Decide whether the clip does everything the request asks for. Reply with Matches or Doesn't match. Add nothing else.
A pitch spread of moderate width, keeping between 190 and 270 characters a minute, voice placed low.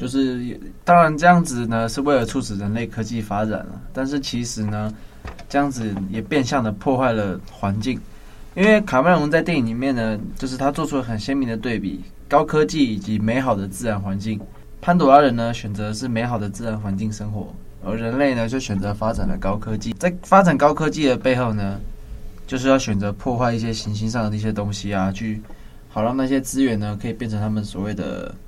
Doesn't match